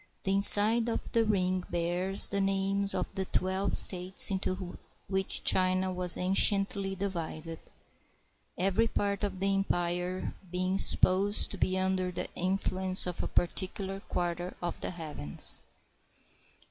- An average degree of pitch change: No, narrow, 1.4 semitones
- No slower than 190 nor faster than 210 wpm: No, slow, 135 wpm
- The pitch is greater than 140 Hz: Yes, high, 190 Hz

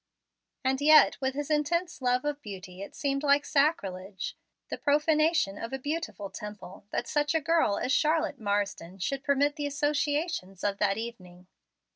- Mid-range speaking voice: No, very high, 275 Hz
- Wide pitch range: Yes, wide, 6.7 semitones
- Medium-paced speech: Yes, average, 160 wpm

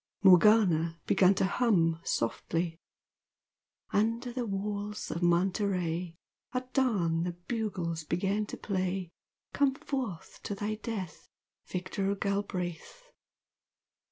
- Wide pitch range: No, average, 3.7 semitones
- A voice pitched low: No, high, 195 Hz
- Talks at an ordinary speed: No, slow, 100 wpm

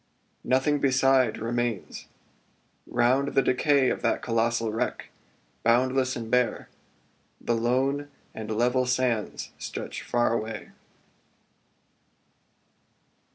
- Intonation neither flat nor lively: No, narrow, 2.2 semitones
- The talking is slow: Yes, slow, 95 wpm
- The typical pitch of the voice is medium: No, low, 125 Hz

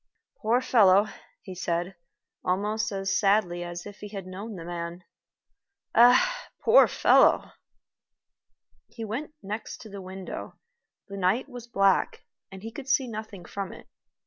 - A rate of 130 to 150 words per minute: Yes, average, 145 wpm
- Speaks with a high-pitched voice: Yes, high, 200 Hz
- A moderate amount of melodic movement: Yes, average, 3.5 semitones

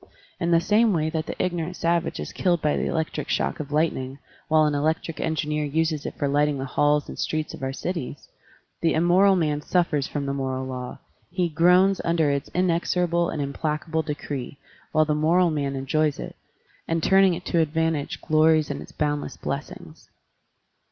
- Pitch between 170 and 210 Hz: No, medium, 155 Hz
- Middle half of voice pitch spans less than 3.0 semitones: Yes, narrow, 2.5 semitones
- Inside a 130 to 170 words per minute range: No, average, 180 wpm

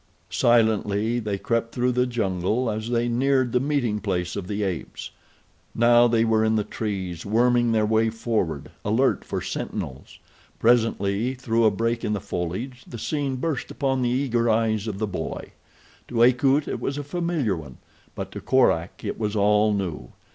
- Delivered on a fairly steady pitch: No, average, 3.2 semitones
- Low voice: Yes, low, 115 Hz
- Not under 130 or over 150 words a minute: No, average, 175 wpm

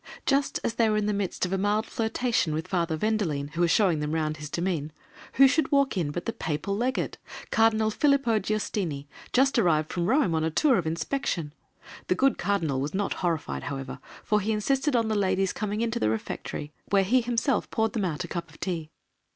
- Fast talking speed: Yes, fast, 210 wpm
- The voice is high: Yes, high, 195 Hz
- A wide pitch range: Yes, wide, 6.0 semitones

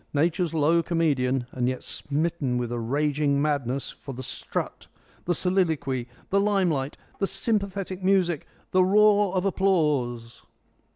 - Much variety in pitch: Yes, wide, 5.7 semitones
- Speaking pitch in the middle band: Yes, medium, 155 Hz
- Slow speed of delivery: Yes, slow, 130 wpm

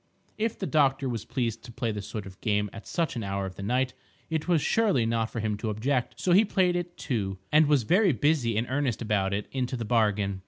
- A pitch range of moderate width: No, wide, 6.1 semitones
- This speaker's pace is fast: Yes, fast, 240 wpm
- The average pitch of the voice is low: Yes, low, 120 Hz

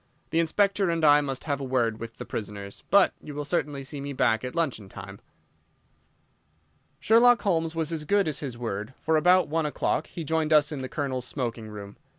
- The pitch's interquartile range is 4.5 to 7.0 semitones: Yes, average, 5.1 semitones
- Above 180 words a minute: Yes, average, 200 wpm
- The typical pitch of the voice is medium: Yes, medium, 145 Hz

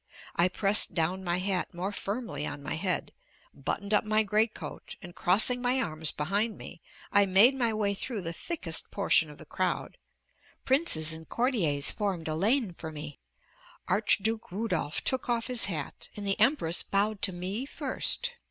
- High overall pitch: Yes, high, 200 Hz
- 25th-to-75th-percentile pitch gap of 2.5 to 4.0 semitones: No, average, 4.6 semitones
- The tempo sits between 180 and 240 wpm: No, average, 170 wpm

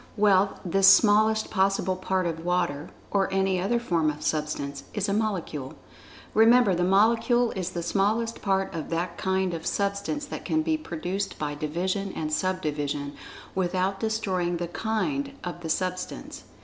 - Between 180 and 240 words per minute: No, average, 160 wpm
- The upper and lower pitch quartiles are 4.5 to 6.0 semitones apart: No, average, 3.3 semitones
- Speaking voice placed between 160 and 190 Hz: Yes, medium, 185 Hz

